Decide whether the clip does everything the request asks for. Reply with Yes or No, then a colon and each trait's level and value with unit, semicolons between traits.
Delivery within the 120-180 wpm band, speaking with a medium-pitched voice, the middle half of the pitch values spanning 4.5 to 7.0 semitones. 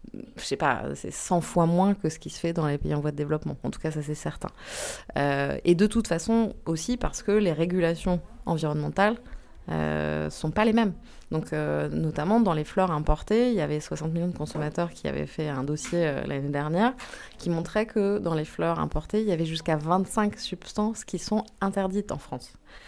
No: average, 215 wpm; medium, 165 Hz; average, 5.0 semitones